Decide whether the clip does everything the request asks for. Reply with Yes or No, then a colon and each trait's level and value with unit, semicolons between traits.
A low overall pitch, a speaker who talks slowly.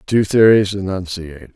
Yes: very low, 95 Hz; slow, 115 wpm